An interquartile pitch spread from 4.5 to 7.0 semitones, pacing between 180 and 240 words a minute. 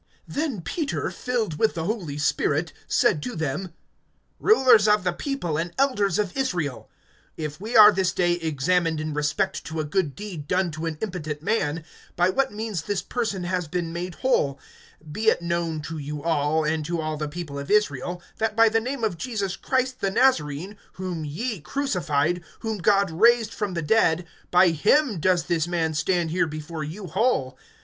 Yes: wide, 5.4 semitones; average, 185 wpm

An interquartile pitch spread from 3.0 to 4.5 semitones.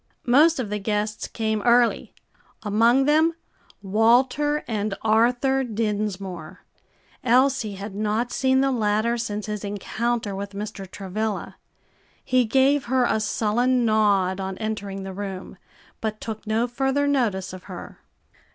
Yes: average, 3.3 semitones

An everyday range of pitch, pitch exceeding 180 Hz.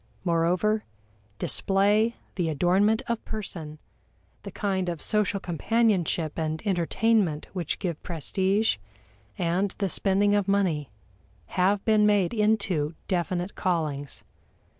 Yes: average, 3.6 semitones; high, 190 Hz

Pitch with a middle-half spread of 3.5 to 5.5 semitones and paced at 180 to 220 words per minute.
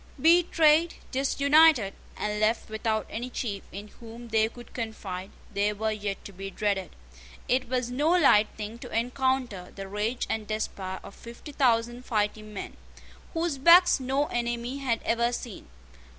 No: average, 3.9 semitones; average, 150 wpm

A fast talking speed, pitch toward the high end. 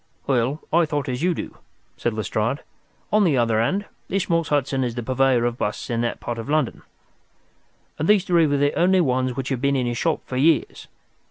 No: fast, 210 wpm; low, 135 Hz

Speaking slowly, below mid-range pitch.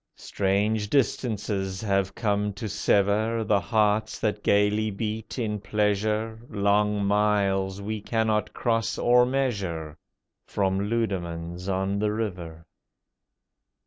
Yes: slow, 110 wpm; low, 105 Hz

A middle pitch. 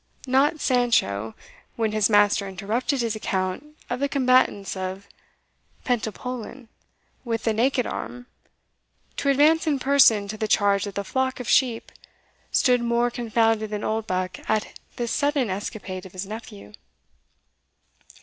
No: high, 225 Hz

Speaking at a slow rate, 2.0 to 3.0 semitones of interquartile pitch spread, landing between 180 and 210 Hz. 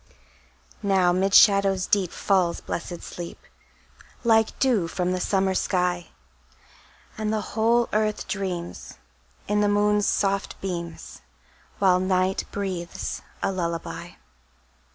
Yes: slow, 110 wpm; narrow, 2.4 semitones; high, 190 Hz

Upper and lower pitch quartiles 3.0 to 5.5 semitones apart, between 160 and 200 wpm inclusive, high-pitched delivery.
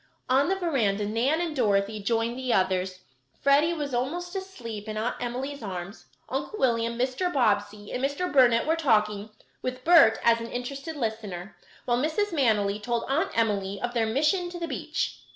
Yes: average, 5.2 semitones; average, 170 wpm; high, 245 Hz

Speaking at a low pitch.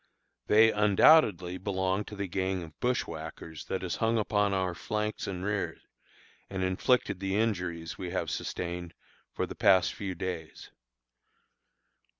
Yes: very low, 95 Hz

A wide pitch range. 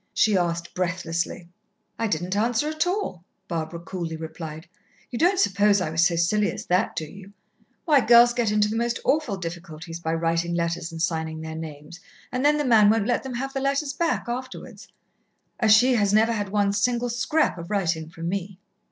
Yes: wide, 6.1 semitones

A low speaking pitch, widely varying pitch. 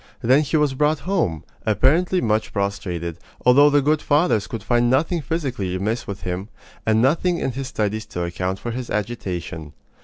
Yes: low, 120 Hz; wide, 6.8 semitones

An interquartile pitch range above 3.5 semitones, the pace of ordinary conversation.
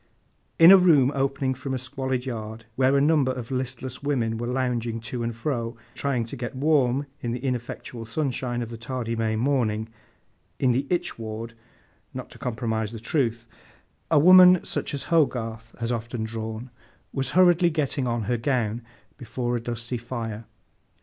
No: average, 3.0 semitones; average, 165 wpm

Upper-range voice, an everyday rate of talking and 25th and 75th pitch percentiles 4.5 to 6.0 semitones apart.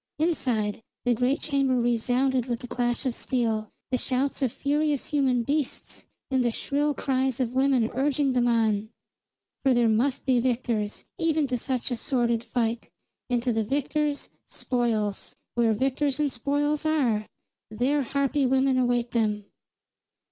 No: very high, 255 Hz; average, 150 wpm; average, 2.9 semitones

